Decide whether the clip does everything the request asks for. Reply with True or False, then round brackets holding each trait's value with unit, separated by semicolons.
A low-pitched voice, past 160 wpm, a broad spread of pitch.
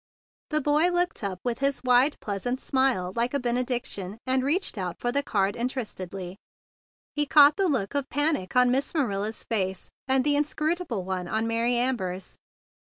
False (250 Hz; 170 wpm; 6.0 semitones)